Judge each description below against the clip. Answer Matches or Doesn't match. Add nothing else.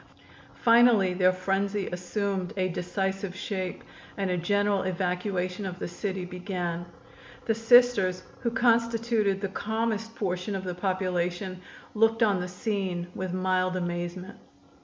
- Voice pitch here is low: Doesn't match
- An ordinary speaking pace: Doesn't match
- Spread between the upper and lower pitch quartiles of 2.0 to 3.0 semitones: Matches